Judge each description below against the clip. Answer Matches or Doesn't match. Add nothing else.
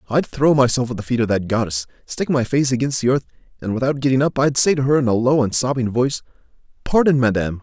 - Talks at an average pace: Doesn't match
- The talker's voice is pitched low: Matches